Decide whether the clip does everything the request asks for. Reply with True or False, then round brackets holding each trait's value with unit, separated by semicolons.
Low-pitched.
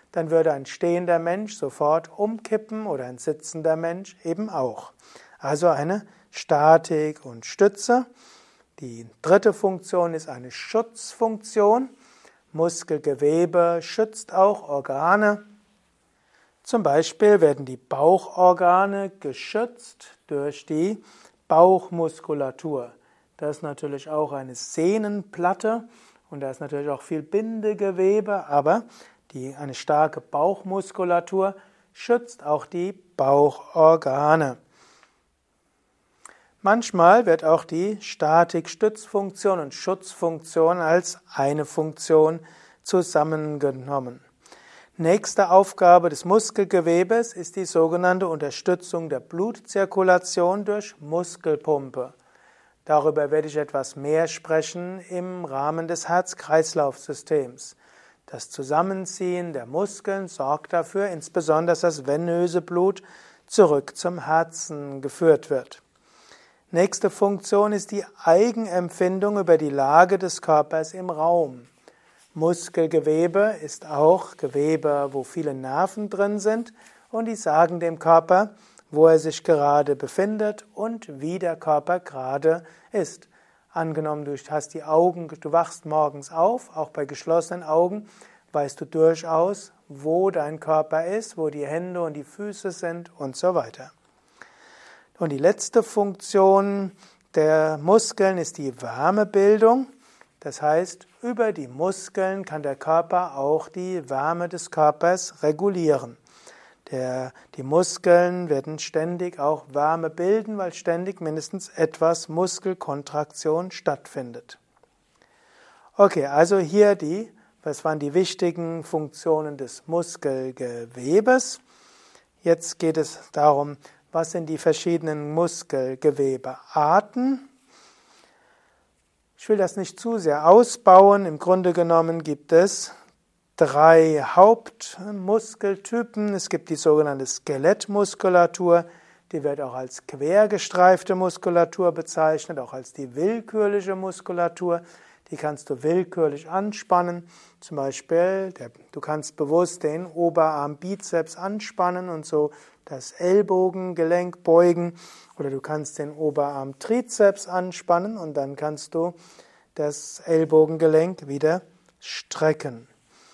False (170 Hz)